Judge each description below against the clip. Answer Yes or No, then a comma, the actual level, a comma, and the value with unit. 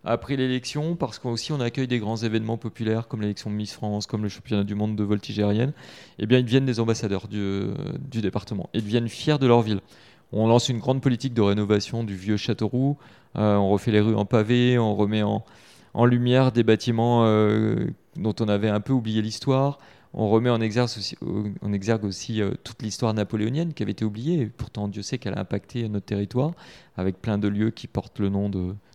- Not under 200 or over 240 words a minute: Yes, fast, 220 wpm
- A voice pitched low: Yes, low, 110 Hz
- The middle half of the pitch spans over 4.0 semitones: No, average, 2.9 semitones